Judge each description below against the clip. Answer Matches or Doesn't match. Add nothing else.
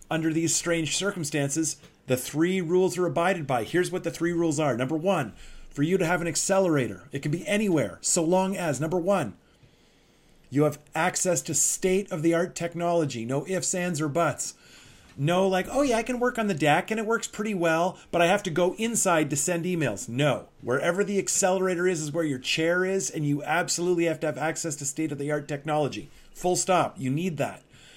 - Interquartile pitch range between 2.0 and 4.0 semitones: Matches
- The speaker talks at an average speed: Doesn't match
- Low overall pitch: Doesn't match